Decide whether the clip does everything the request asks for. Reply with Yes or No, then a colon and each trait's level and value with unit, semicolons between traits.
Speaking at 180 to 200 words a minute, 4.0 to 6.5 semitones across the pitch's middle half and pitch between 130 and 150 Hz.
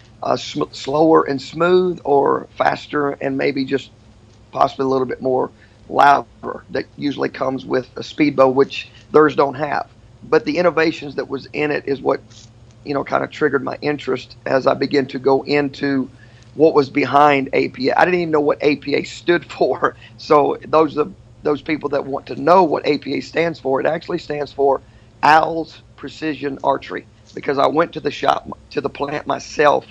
No: average, 185 wpm; narrow, 2.4 semitones; medium, 140 Hz